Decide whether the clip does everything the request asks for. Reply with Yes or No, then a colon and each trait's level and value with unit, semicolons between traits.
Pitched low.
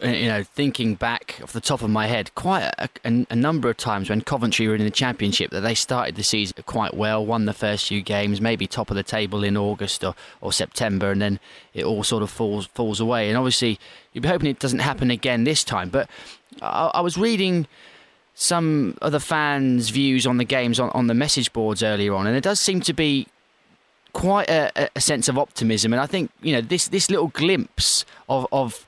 Yes: low, 120 Hz